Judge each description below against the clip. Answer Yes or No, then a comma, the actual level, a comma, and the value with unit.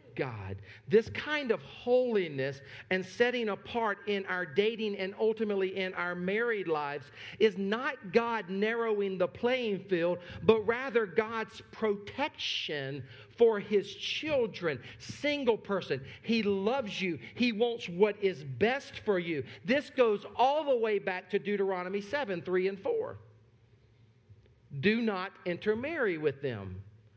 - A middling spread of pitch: Yes, average, 4.9 semitones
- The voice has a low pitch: No, high, 200 Hz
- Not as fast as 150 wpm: Yes, slow, 135 wpm